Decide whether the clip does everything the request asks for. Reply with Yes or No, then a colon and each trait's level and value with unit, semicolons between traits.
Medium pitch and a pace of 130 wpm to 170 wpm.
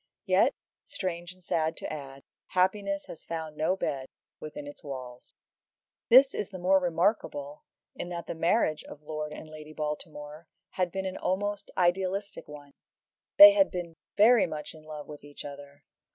Yes: medium, 165 Hz; average, 165 wpm